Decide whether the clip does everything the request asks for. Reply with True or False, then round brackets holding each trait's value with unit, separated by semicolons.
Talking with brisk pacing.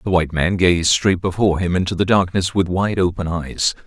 True (215 wpm)